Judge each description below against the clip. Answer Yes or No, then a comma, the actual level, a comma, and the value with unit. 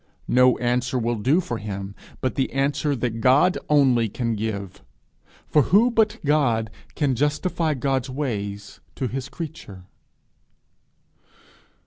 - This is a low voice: Yes, low, 130 Hz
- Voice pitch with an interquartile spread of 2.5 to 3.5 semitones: No, average, 4.6 semitones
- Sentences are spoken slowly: Yes, slow, 125 wpm